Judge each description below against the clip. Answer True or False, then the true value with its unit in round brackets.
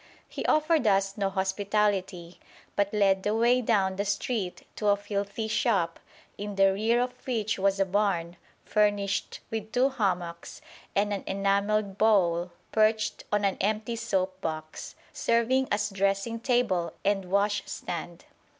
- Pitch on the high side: True (200 Hz)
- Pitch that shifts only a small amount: True (2.1 semitones)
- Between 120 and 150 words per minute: True (140 wpm)